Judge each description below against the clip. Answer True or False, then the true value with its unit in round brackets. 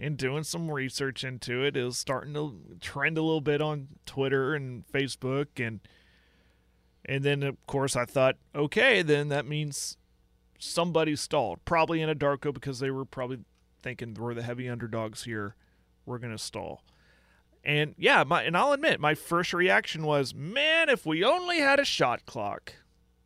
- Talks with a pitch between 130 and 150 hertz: True (140 Hz)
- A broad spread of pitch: False (3.9 semitones)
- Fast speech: False (175 wpm)